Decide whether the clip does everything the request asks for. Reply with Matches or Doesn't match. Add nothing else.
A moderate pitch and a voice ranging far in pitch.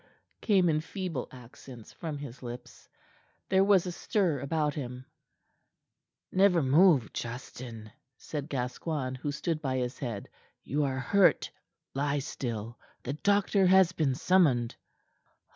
Matches